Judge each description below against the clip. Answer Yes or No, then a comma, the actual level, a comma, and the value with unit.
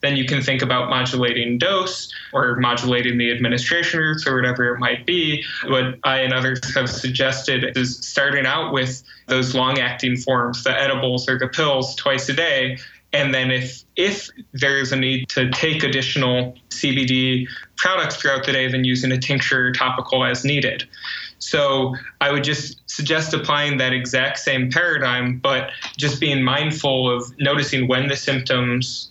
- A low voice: Yes, low, 130 Hz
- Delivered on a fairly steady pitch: Yes, narrow, 1.8 semitones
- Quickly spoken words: No, average, 170 wpm